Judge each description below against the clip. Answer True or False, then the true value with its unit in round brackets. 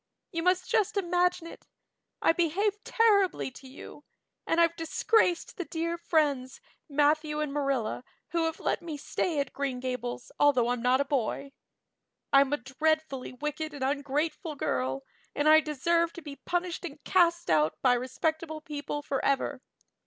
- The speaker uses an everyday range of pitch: True (3.7 semitones)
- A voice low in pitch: False (300 Hz)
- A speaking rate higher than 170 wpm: False (155 wpm)